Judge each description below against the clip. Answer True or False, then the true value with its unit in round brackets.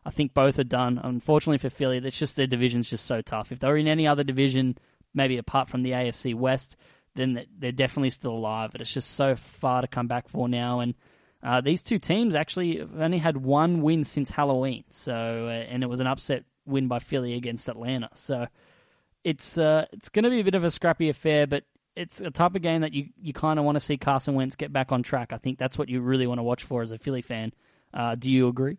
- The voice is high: False (135 Hz)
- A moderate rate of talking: False (245 wpm)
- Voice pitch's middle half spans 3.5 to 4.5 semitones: False (3.1 semitones)